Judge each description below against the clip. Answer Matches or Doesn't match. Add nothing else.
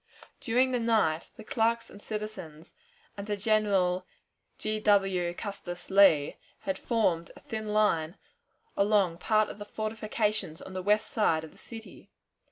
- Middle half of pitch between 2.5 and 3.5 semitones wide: Matches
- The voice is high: Matches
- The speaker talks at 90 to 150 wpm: Matches